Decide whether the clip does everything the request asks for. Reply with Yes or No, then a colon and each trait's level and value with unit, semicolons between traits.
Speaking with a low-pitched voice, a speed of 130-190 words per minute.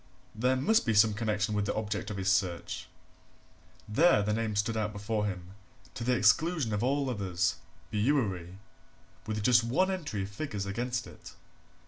Yes: low, 110 Hz; average, 165 wpm